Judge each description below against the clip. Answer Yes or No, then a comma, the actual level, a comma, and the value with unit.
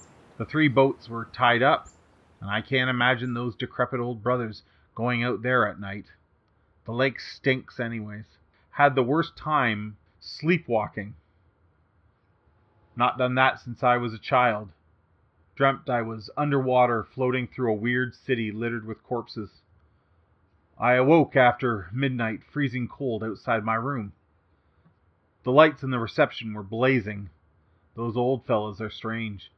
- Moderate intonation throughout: Yes, average, 4.2 semitones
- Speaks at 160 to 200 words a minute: No, average, 140 wpm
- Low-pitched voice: Yes, low, 115 Hz